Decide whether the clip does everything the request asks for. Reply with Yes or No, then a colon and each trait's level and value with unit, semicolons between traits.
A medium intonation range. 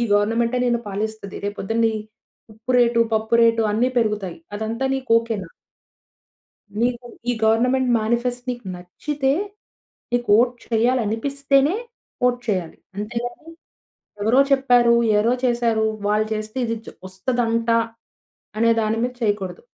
No: narrow, 2.2 semitones